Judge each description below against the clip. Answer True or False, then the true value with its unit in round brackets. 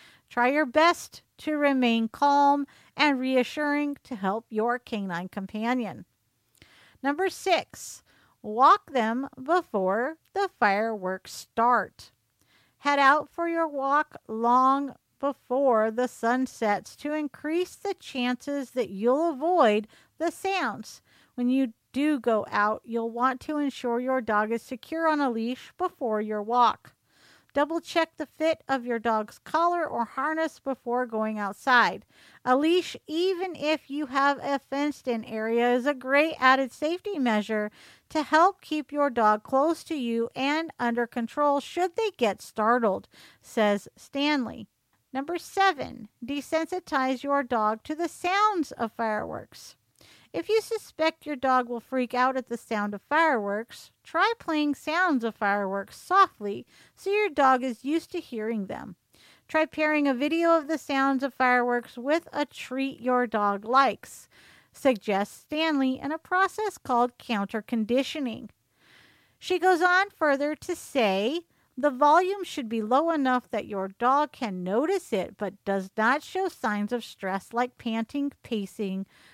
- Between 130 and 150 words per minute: True (145 wpm)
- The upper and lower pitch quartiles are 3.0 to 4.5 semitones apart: False (5.1 semitones)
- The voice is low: False (265 Hz)